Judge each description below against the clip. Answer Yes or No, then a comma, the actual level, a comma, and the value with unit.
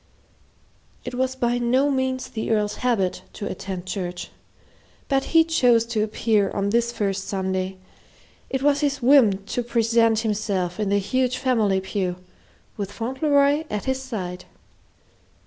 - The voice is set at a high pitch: Yes, high, 225 Hz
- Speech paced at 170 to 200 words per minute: No, average, 145 wpm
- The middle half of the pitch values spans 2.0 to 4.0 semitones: No, average, 4.7 semitones